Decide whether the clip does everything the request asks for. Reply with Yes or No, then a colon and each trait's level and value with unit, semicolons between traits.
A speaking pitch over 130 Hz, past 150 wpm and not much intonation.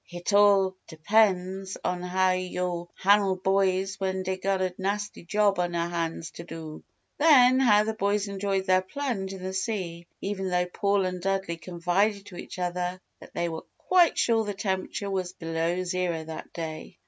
Yes: high, 190 Hz; average, 170 wpm; narrow, 2.1 semitones